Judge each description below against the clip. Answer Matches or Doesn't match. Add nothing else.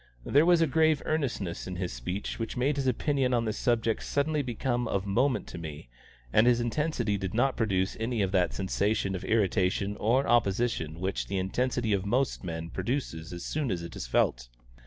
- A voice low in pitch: Matches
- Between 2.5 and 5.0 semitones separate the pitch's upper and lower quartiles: Doesn't match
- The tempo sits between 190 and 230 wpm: Matches